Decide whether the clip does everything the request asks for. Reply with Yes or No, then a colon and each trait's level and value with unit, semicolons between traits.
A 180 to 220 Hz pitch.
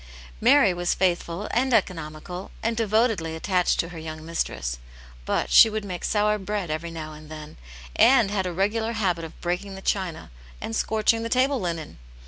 Yes: medium, 185 Hz